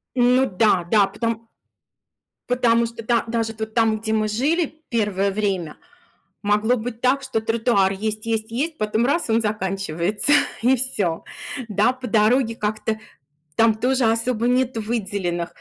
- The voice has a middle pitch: No, high, 225 Hz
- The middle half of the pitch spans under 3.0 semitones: Yes, narrow, 2.6 semitones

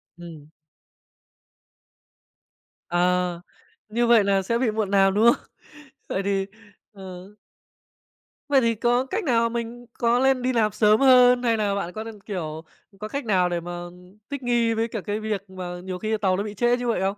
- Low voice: No, high, 215 Hz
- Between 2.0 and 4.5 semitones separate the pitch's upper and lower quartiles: Yes, average, 3.9 semitones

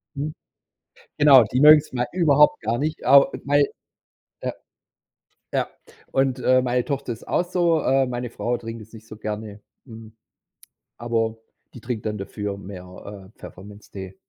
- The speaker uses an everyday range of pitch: Yes, average, 4.4 semitones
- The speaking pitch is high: No, low, 120 Hz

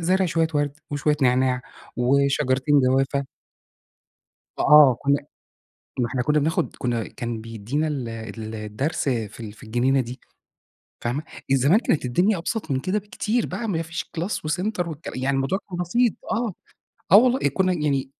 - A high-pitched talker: No, medium, 140 Hz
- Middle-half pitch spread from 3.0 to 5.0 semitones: No, wide, 5.5 semitones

